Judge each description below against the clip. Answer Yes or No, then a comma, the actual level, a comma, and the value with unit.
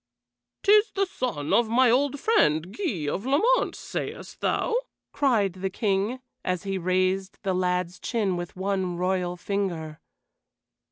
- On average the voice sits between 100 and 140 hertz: No, high, 195 Hz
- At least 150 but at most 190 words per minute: No, slow, 135 wpm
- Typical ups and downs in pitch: No, wide, 5.7 semitones